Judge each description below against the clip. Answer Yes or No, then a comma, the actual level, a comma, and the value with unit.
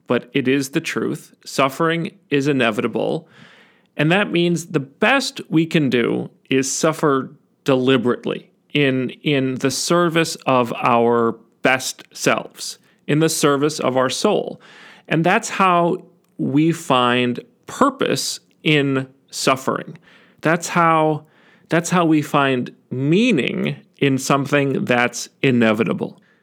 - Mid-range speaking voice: Yes, medium, 150 Hz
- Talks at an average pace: No, slow, 120 wpm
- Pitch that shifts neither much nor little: Yes, average, 4.3 semitones